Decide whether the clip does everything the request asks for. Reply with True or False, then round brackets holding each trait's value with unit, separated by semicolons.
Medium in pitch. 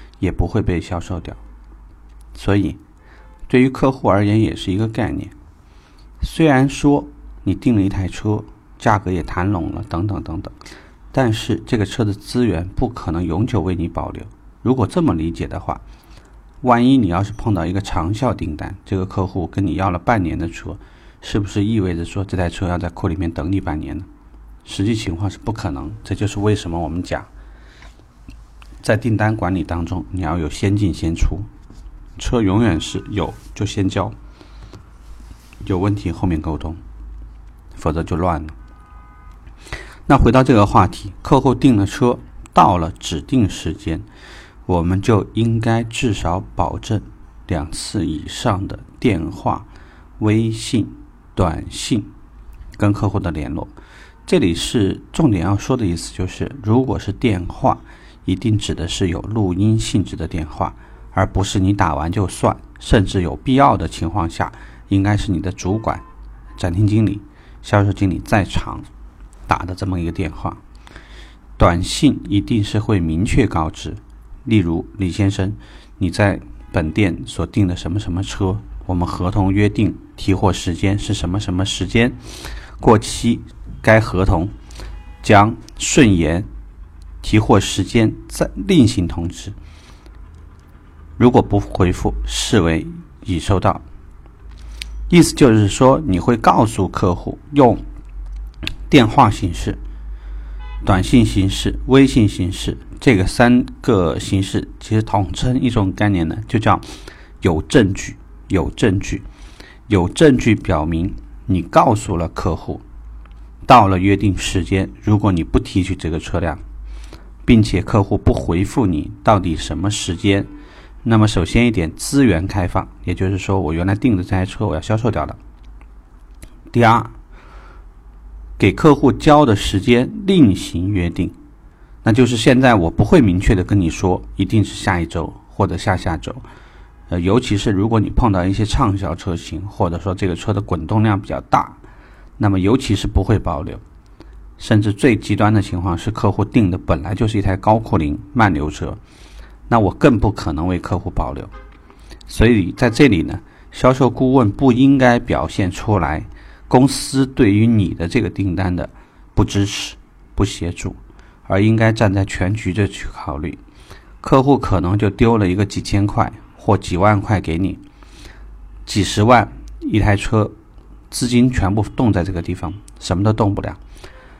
False (95 Hz)